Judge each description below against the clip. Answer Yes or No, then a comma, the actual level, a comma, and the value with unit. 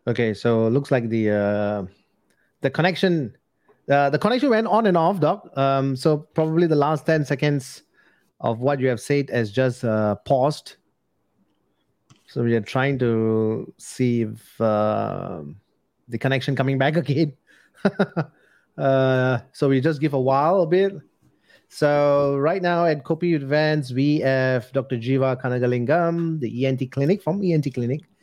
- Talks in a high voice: No, low, 135 Hz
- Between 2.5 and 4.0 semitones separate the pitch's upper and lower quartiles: No, average, 4.5 semitones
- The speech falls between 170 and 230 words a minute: No, average, 155 wpm